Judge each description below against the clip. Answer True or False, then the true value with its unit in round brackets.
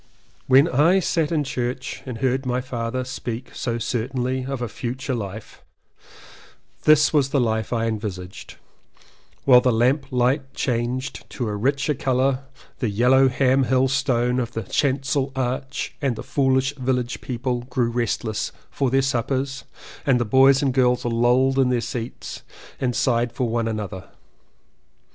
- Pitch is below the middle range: True (125 Hz)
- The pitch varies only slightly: True (2.0 semitones)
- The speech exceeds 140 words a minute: True (155 wpm)